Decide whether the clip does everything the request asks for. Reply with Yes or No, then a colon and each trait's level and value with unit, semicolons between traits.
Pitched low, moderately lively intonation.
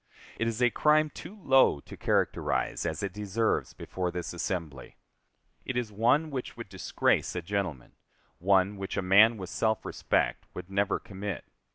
Yes: low, 100 Hz; average, 3.9 semitones